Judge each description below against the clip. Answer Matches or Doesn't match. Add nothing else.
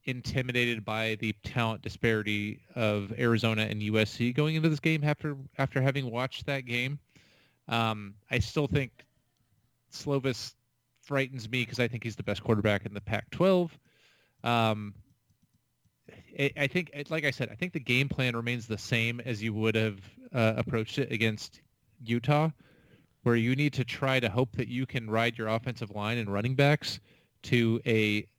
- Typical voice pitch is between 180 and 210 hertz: Doesn't match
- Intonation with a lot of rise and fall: Doesn't match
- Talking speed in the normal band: Matches